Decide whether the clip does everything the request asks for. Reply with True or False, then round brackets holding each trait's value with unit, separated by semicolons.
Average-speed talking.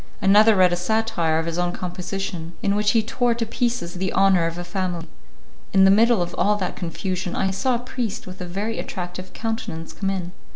False (210 wpm)